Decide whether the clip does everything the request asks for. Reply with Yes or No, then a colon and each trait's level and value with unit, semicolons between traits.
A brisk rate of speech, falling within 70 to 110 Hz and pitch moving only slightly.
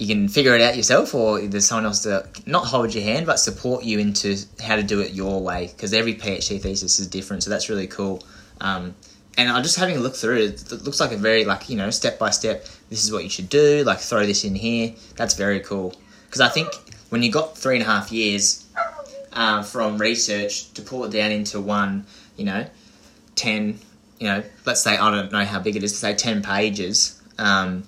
Yes: fast, 235 wpm; low, 105 Hz; narrow, 2.3 semitones